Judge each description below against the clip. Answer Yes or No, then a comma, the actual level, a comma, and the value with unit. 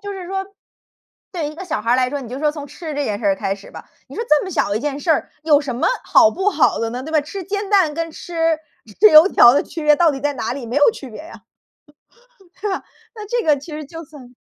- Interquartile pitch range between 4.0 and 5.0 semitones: Yes, average, 4.5 semitones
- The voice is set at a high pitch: Yes, very high, 300 Hz